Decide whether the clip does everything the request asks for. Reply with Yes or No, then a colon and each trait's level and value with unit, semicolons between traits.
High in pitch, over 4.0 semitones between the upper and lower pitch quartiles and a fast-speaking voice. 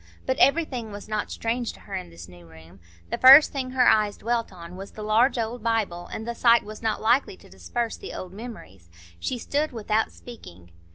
Yes: high, 220 Hz; average, 4.5 semitones; fast, 210 wpm